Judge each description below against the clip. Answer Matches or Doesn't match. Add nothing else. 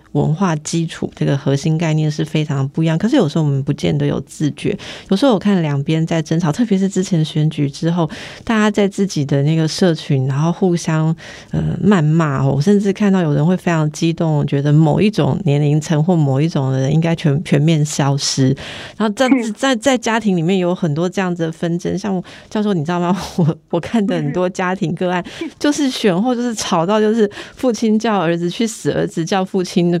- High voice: Doesn't match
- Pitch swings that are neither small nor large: Matches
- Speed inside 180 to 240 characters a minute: Doesn't match